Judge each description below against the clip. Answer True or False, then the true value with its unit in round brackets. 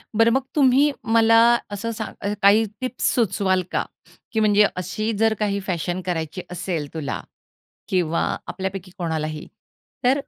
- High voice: True (200 Hz)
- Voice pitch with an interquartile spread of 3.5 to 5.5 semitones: True (4.2 semitones)